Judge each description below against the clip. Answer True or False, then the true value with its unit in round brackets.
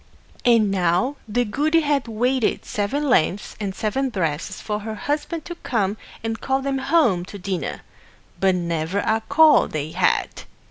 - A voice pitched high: True (220 Hz)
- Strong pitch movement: True (6.0 semitones)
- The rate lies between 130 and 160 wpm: True (155 wpm)